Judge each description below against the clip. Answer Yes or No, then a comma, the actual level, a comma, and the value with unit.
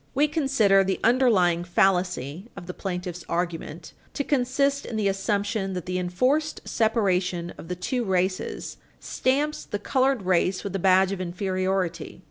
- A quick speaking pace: No, average, 150 wpm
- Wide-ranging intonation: No, average, 4.8 semitones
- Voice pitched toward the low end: No, high, 195 Hz